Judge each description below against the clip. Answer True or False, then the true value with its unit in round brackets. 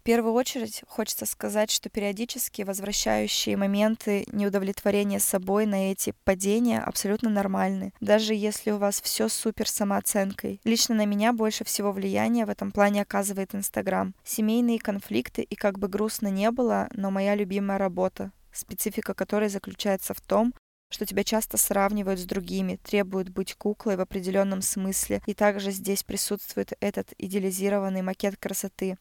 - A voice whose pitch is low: False (205 Hz)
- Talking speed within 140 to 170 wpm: True (145 wpm)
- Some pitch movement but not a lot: False (1.7 semitones)